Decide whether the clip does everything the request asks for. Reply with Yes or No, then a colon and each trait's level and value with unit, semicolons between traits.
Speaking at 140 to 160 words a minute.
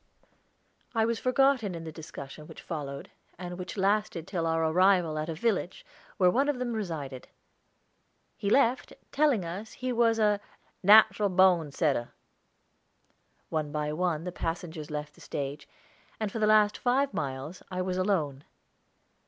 Yes: average, 155 wpm